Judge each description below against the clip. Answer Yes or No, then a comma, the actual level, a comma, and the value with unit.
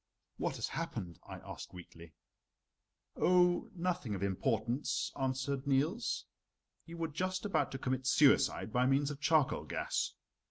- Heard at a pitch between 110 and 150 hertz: Yes, low, 135 Hz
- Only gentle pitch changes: No, average, 5.0 semitones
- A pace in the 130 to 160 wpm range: Yes, slow, 135 wpm